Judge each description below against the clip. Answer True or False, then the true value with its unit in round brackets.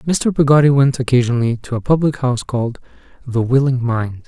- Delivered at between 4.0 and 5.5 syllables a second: False (5.8 syllables/s)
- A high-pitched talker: False (130 Hz)